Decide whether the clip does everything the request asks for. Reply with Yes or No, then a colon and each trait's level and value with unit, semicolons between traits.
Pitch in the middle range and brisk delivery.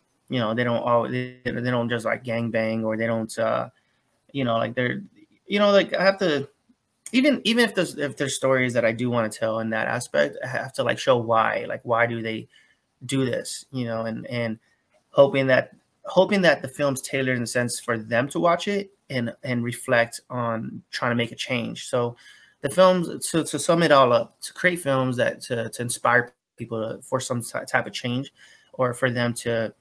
No: low, 125 Hz; fast, 220 wpm